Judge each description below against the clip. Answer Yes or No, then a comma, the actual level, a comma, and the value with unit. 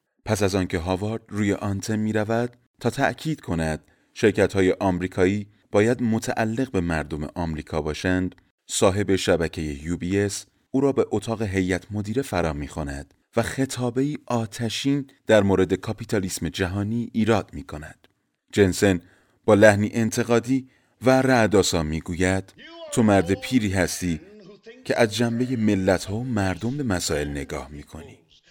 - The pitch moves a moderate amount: Yes, average, 4.5 semitones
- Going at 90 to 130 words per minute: No, average, 140 wpm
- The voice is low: Yes, low, 105 Hz